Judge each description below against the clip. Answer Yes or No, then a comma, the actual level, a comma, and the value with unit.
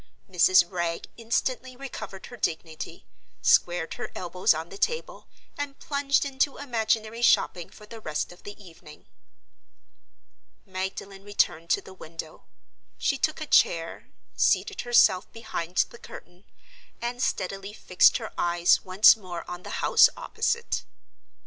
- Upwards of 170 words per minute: No, slow, 135 wpm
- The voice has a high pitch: Yes, high, 195 Hz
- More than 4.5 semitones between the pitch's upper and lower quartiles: Yes, wide, 5.6 semitones